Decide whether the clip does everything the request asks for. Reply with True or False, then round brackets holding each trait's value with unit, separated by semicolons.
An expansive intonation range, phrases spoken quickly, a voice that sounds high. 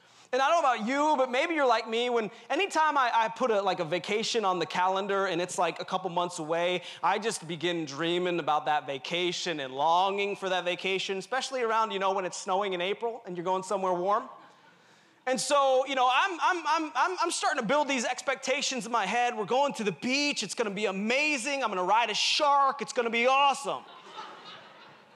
True (6.4 semitones; 220 wpm; 220 Hz)